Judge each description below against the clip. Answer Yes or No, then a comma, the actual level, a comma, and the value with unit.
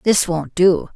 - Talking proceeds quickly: No, average, 190 wpm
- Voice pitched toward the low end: No, medium, 180 Hz